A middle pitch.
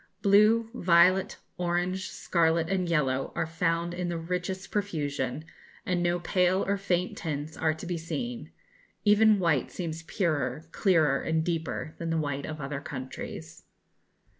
Yes: medium, 170 Hz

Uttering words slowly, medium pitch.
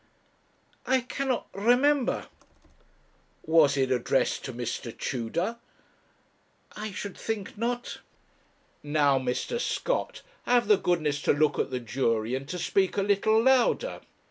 Yes: slow, 125 wpm; medium, 180 Hz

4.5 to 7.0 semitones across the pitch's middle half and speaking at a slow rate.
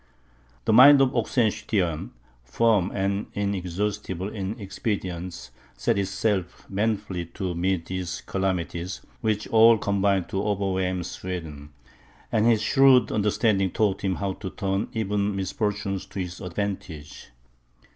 No: narrow, 2.4 semitones; slow, 120 wpm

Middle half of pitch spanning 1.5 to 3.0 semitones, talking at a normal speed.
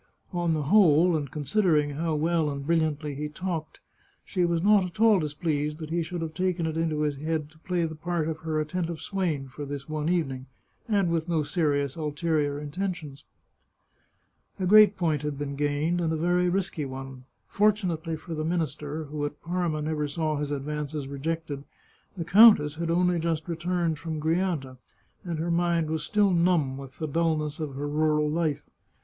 Yes: narrow, 2.6 semitones; average, 180 wpm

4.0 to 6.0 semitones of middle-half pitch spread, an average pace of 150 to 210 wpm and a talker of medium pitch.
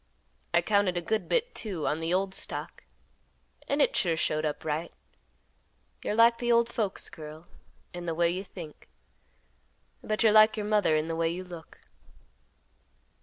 Yes: average, 4.8 semitones; average, 170 wpm; medium, 180 Hz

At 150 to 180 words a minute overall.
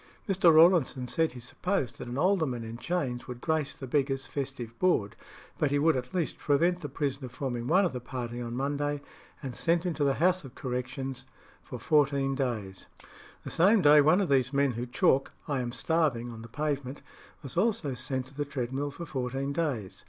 No: average, 195 wpm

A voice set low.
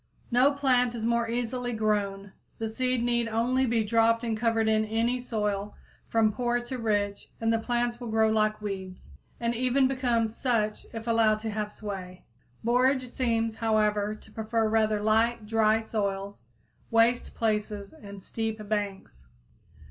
No: high, 225 Hz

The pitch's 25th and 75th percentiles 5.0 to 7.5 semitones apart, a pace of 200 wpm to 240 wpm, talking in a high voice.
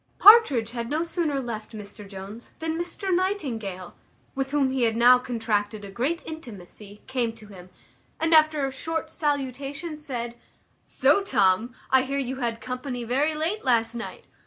No: average, 5.3 semitones; average, 160 wpm; very high, 255 Hz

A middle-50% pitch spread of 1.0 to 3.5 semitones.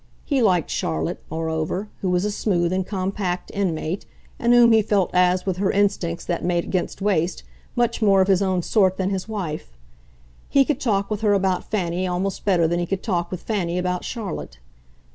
Yes: narrow, 2.6 semitones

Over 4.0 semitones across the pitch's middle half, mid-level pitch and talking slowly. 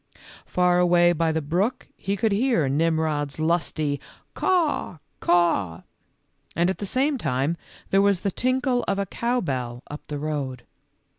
No: wide, 5.4 semitones; medium, 175 Hz; average, 155 wpm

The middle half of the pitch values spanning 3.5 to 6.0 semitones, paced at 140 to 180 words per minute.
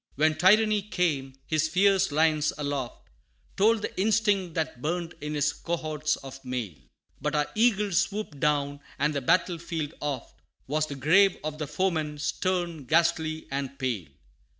Yes: average, 4.2 semitones; average, 155 wpm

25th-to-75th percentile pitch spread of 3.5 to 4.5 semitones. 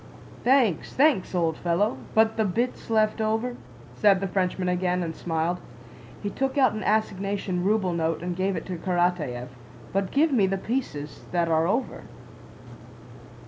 Yes: average, 3.9 semitones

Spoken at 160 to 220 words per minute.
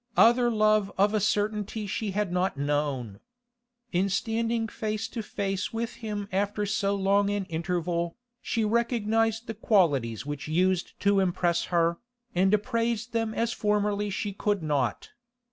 No: average, 145 wpm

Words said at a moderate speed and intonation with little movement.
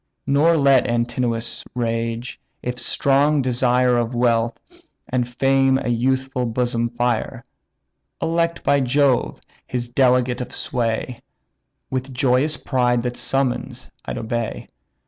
No: slow, 115 wpm; narrow, 2.0 semitones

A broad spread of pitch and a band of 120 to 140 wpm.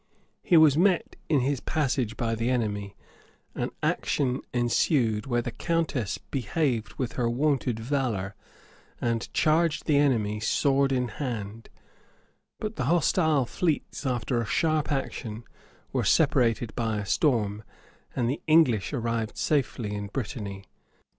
No: average, 4.5 semitones; slow, 135 wpm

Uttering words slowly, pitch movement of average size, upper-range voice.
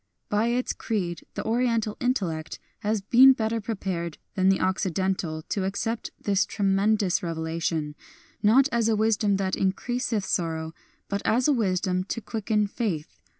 No: average, 145 wpm; average, 3.5 semitones; high, 200 Hz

